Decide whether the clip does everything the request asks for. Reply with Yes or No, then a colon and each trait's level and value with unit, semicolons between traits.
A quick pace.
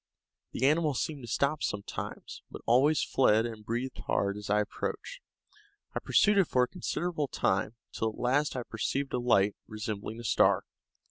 No: average, 175 wpm